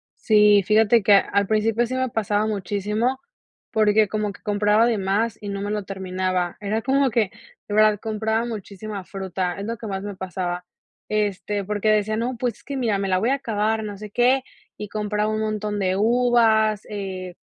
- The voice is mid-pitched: No, high, 210 Hz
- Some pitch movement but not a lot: No, narrow, 1.9 semitones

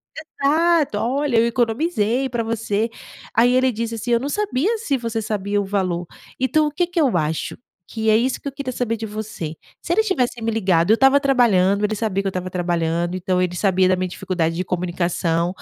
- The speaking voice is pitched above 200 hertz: Yes, high, 220 Hz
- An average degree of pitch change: No, wide, 5.9 semitones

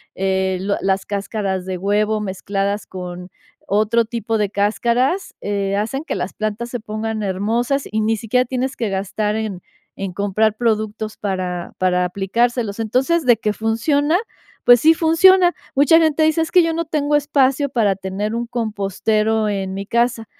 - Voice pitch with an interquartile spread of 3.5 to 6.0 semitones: Yes, average, 3.9 semitones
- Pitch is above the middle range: Yes, high, 215 Hz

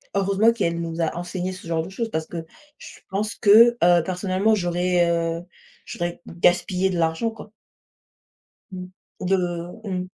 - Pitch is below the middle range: No, medium, 180 Hz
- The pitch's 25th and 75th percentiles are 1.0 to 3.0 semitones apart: Yes, narrow, 2.5 semitones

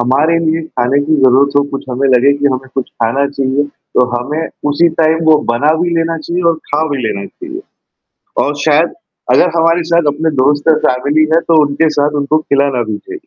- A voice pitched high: No, medium, 145 Hz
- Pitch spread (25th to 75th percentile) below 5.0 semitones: Yes, average, 3.2 semitones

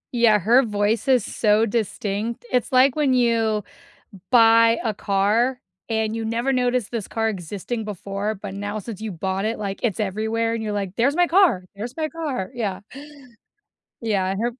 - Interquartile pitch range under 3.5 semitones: Yes, average, 2.9 semitones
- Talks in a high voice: Yes, high, 220 Hz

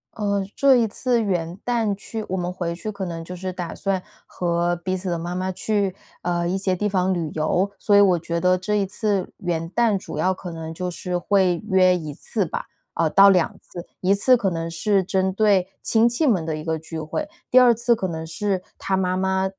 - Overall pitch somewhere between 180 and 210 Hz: Yes, medium, 185 Hz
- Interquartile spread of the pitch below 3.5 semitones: Yes, average, 2.7 semitones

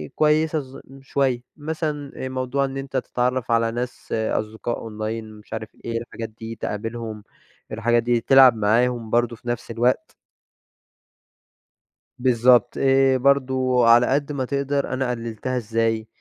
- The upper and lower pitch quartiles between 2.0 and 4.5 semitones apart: Yes, average, 2.7 semitones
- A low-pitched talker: Yes, low, 120 Hz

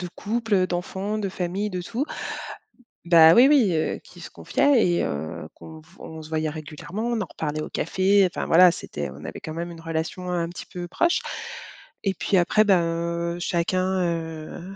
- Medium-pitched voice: Yes, medium, 175 Hz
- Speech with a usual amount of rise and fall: Yes, average, 3.1 semitones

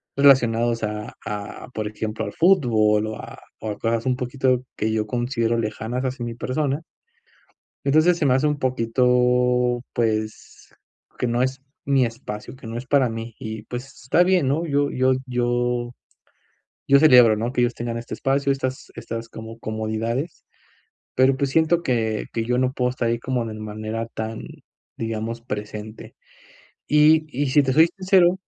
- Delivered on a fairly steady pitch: No, average, 3.1 semitones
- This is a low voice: Yes, low, 120 Hz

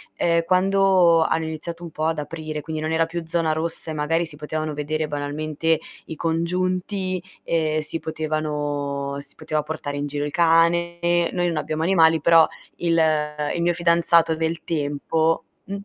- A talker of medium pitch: Yes, medium, 160 Hz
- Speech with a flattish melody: Yes, narrow, 1.6 semitones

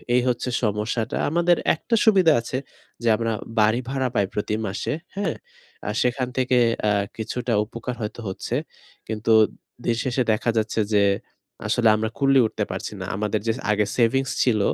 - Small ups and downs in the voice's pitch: No, average, 3.4 semitones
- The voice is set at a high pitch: No, low, 115 Hz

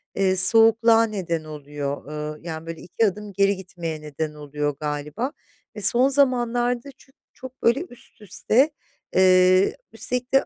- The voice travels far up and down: Yes, wide, 7.2 semitones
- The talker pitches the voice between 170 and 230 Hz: Yes, high, 190 Hz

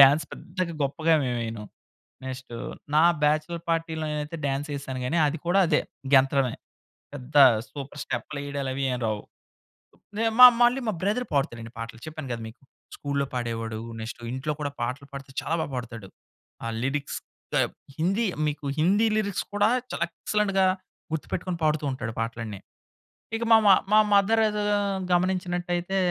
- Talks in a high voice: No, medium, 150 Hz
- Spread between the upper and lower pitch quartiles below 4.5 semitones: No, average, 5.3 semitones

